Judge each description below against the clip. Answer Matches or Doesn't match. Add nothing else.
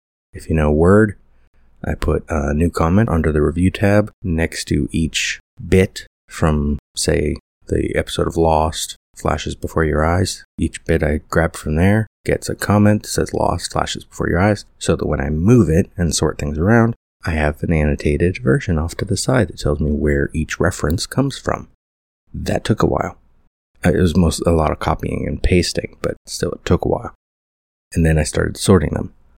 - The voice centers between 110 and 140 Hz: Doesn't match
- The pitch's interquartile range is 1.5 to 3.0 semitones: Doesn't match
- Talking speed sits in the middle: Matches